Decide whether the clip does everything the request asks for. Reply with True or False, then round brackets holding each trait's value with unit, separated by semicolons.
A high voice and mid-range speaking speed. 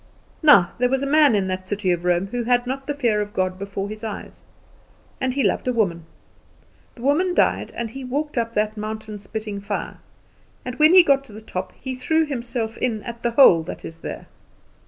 False (230 Hz; 215 wpm)